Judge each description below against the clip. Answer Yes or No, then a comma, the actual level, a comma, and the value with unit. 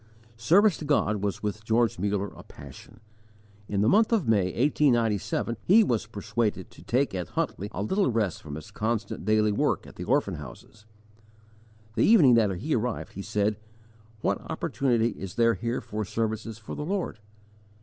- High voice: No, low, 110 Hz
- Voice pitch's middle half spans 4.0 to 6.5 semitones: No, average, 3.2 semitones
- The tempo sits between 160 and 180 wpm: Yes, average, 170 wpm